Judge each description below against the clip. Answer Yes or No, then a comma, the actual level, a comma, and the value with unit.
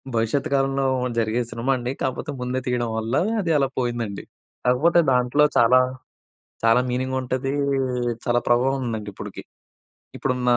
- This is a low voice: Yes, low, 125 Hz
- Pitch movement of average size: No, narrow, 2.1 semitones